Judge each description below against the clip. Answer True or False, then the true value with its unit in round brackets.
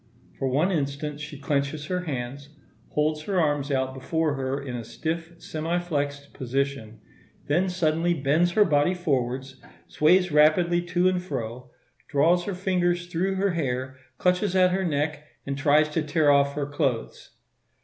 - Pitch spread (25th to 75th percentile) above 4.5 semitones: False (3.9 semitones)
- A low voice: False (150 Hz)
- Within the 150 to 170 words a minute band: True (160 wpm)